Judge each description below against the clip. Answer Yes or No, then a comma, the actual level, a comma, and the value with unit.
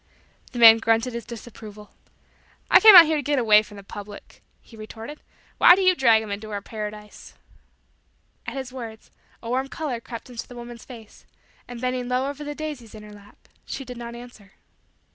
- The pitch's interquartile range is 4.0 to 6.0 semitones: No, average, 3.2 semitones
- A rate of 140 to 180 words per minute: No, average, 195 wpm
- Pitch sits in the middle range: No, high, 235 Hz